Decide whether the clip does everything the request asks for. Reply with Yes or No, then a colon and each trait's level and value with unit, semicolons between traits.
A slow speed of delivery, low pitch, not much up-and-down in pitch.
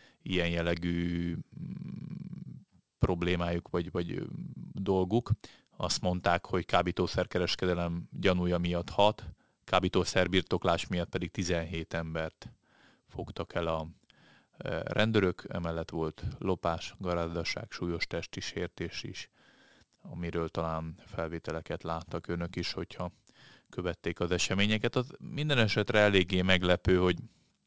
Yes: slow, 100 wpm; very low, 90 Hz; narrow, 2.0 semitones